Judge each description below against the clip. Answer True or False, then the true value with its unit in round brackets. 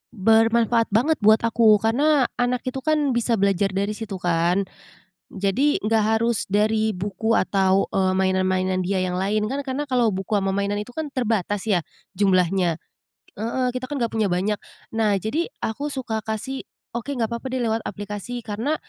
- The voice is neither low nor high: False (220 Hz)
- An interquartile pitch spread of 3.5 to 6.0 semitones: True (3.8 semitones)